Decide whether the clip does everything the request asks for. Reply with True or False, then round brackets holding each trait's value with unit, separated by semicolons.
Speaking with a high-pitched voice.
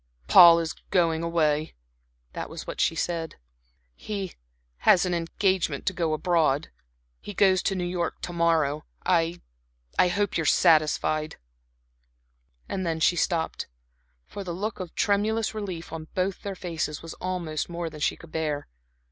False (170 Hz)